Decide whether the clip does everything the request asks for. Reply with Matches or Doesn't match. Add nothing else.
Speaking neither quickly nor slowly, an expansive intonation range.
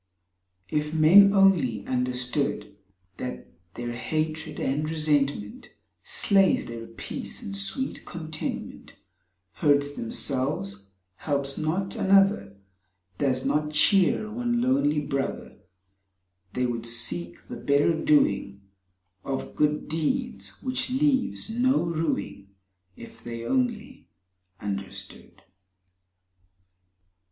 Doesn't match